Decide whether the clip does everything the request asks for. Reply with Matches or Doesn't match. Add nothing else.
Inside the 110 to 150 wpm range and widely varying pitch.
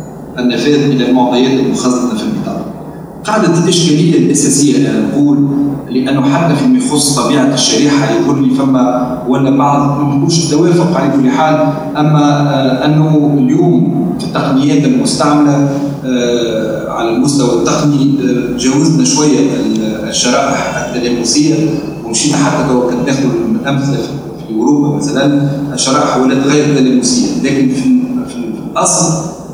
Doesn't match